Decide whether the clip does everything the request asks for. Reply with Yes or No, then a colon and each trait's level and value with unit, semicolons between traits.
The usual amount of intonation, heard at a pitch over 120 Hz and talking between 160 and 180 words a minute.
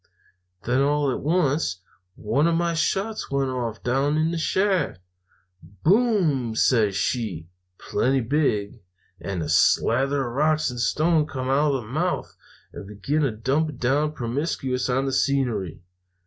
No: average, 4.6 semitones; low, 135 Hz; average, 150 wpm